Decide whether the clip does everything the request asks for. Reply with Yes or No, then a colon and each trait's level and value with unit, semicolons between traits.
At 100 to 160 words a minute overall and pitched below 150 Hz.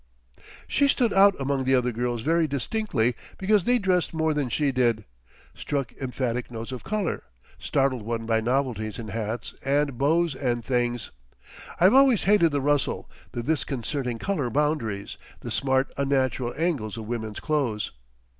Yes: average, 155 wpm; low, 135 Hz